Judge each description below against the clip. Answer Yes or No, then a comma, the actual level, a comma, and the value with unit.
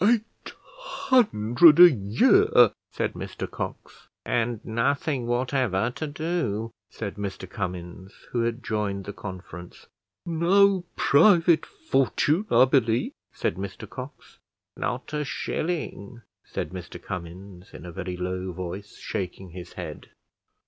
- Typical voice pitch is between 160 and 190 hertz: No, low, 115 Hz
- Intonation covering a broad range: Yes, wide, 8.7 semitones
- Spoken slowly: Yes, slow, 120 wpm